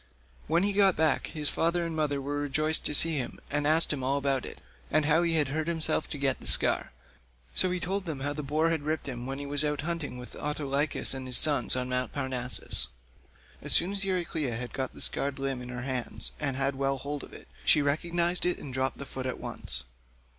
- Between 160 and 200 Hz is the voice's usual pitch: No, medium, 145 Hz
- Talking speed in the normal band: No, fast, 235 wpm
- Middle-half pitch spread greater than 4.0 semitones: No, average, 3.2 semitones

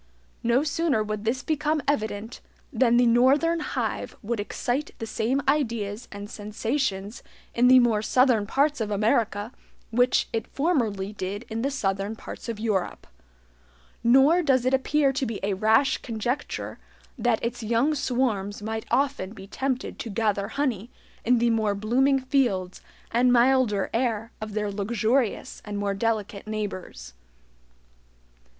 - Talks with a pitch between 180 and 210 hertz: No, high, 230 Hz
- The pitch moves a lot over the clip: No, average, 3.9 semitones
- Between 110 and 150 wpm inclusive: Yes, average, 145 wpm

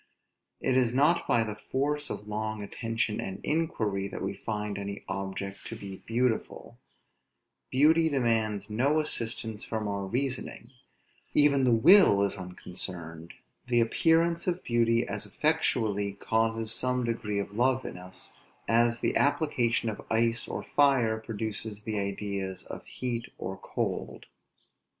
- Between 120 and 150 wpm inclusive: Yes, average, 140 wpm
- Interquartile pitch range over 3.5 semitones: Yes, average, 3.9 semitones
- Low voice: Yes, low, 115 Hz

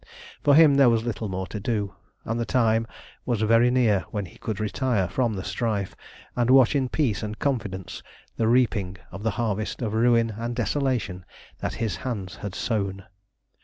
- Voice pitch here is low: Yes, low, 115 Hz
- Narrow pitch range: No, average, 3.2 semitones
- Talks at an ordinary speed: Yes, average, 180 wpm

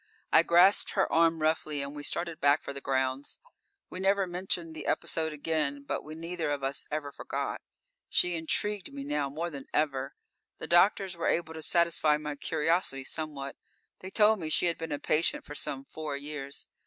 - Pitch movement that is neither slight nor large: Yes, average, 3.1 semitones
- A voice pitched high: No, medium, 155 Hz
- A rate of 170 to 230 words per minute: Yes, average, 190 wpm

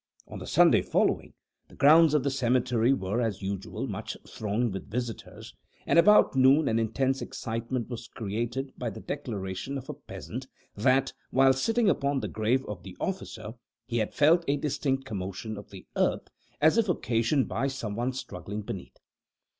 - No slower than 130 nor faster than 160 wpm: No, average, 170 wpm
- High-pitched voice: No, low, 125 Hz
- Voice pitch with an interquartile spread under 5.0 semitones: Yes, average, 3.9 semitones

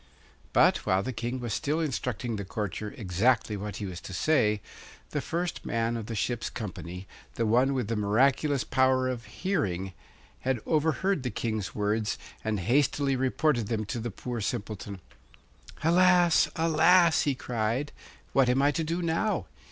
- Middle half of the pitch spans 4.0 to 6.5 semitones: Yes, wide, 5.5 semitones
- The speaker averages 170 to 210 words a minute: No, average, 160 wpm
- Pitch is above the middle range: No, low, 120 Hz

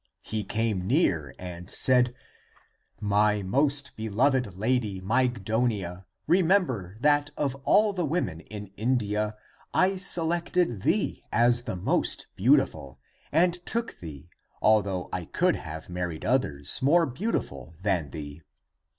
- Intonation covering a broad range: Yes, wide, 7.8 semitones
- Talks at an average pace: No, slow, 125 wpm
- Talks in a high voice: No, low, 110 Hz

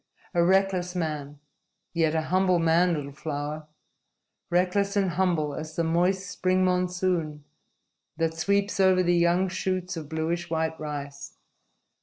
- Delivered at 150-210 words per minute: No, slow, 135 wpm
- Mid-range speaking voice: Yes, medium, 170 Hz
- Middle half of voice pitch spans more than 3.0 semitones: No, narrow, 2.6 semitones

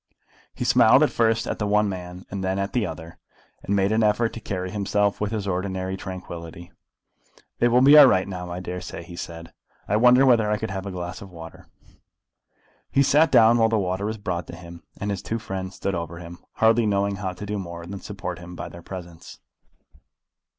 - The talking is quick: Yes, fast, 215 wpm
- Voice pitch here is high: No, very low, 95 Hz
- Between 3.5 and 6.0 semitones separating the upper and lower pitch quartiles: No, average, 3.0 semitones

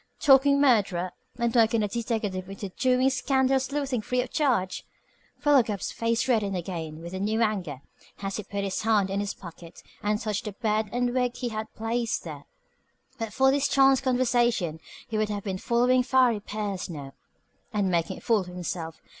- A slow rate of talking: No, average, 180 wpm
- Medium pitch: No, high, 215 Hz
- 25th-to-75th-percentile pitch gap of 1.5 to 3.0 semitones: No, average, 4.5 semitones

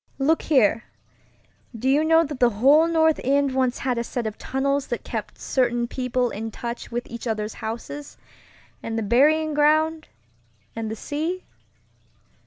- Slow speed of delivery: No, average, 155 wpm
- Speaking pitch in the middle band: No, very high, 260 Hz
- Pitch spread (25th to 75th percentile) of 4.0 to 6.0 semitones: Yes, average, 4.3 semitones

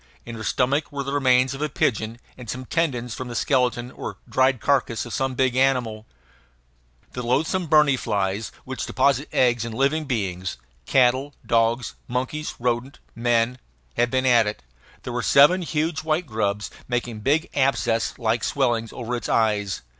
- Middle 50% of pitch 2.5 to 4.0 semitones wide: Yes, average, 3.0 semitones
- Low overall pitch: Yes, low, 125 Hz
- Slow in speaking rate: No, average, 165 wpm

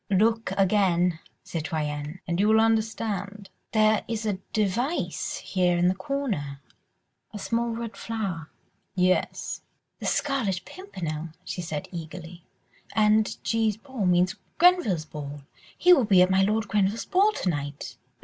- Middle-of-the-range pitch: No, high, 195 Hz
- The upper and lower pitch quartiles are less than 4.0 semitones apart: No, average, 4.3 semitones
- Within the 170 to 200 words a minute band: No, average, 140 wpm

